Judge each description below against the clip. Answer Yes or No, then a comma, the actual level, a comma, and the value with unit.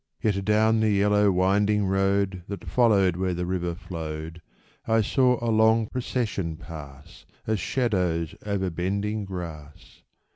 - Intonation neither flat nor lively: Yes, average, 3.4 semitones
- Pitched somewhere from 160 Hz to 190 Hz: No, very low, 95 Hz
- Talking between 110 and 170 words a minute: Yes, slow, 135 wpm